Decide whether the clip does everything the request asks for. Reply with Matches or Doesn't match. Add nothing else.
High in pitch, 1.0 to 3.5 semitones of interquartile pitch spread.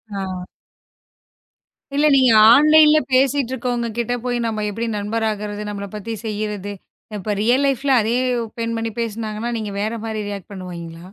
Matches